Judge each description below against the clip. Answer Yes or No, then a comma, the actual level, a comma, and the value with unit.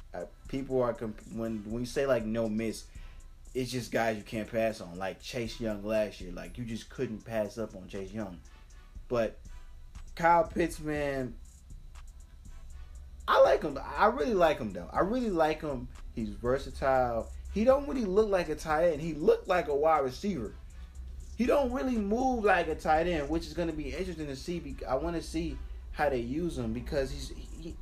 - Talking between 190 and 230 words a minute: Yes, average, 195 wpm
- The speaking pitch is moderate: No, low, 115 Hz